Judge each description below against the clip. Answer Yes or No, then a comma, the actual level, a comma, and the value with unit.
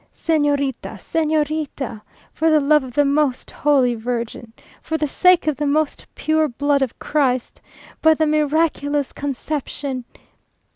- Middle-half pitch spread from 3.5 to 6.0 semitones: No, narrow, 2.5 semitones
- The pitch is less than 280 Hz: No, very high, 290 Hz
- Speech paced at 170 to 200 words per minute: No, slow, 135 wpm